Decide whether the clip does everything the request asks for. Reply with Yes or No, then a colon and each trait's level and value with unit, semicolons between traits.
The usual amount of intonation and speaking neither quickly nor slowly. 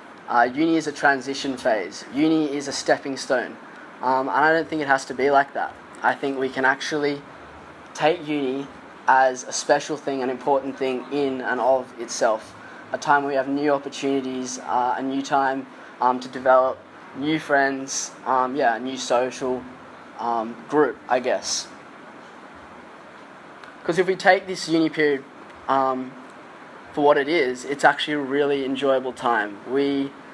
No: narrow, 2.0 semitones; average, 165 wpm